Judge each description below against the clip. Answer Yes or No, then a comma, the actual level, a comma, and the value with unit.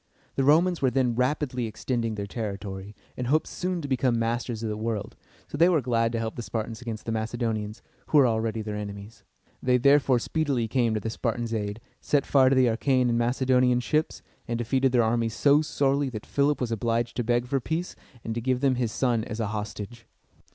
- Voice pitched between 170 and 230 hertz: No, low, 120 Hz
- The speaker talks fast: Yes, fast, 210 wpm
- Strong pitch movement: No, average, 2.8 semitones